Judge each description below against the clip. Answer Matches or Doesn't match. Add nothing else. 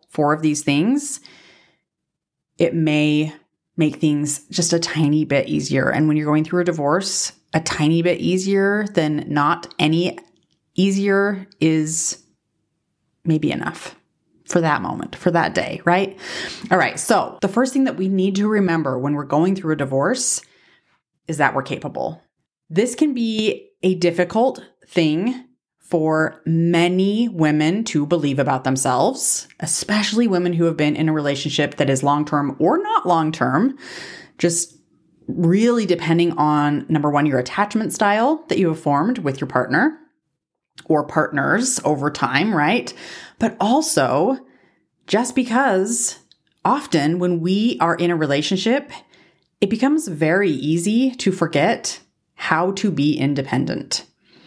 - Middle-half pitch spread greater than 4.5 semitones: Matches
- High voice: Doesn't match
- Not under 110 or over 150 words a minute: Matches